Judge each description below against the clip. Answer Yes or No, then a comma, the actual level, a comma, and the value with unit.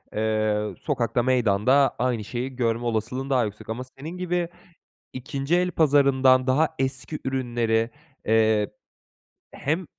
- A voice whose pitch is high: No, low, 130 Hz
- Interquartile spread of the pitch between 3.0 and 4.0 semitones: Yes, average, 3.5 semitones